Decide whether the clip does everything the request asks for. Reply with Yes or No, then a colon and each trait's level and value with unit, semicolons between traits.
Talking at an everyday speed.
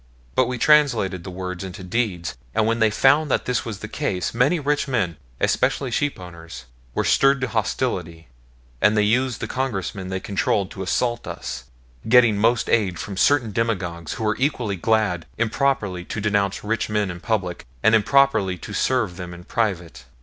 Yes: average, 180 wpm